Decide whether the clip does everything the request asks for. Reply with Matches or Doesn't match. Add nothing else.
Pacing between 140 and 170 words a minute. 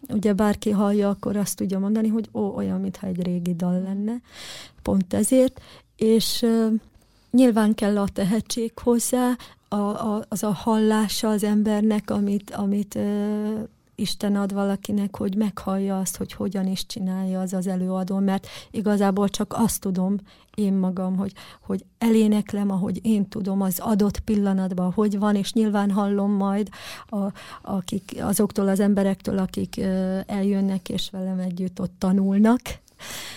Matches